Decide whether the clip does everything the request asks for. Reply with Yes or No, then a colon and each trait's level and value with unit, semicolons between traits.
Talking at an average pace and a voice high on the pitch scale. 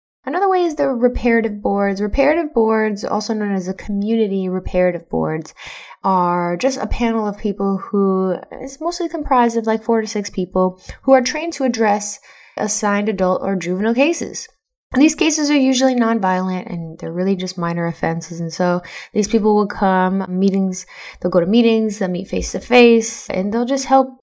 Yes: average, 180 wpm; high, 210 Hz